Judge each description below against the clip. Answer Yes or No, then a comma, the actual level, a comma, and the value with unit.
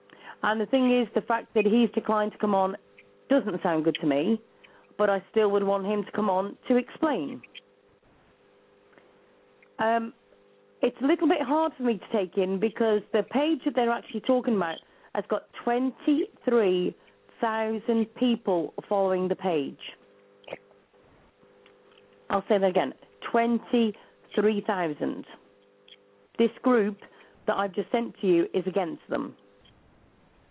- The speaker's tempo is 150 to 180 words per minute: No, average, 140 wpm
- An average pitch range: Yes, average, 3.7 semitones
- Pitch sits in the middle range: No, high, 215 Hz